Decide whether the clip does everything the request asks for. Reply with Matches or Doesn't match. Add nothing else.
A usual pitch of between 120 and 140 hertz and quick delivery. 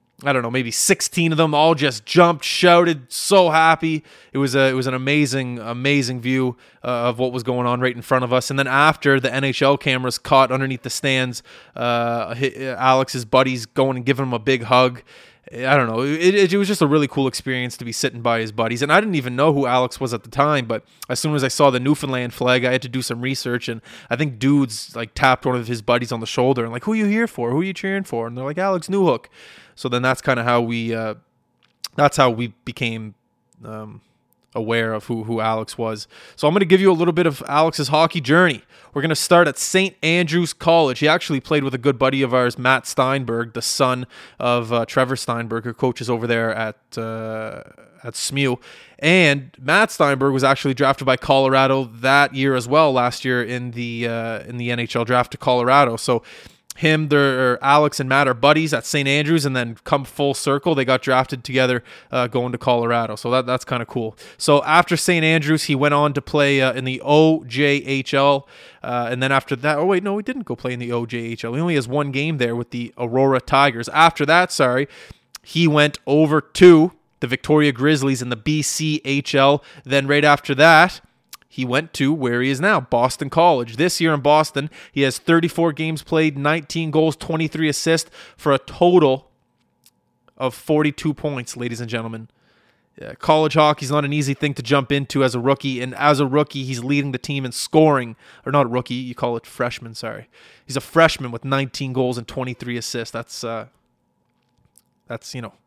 Matches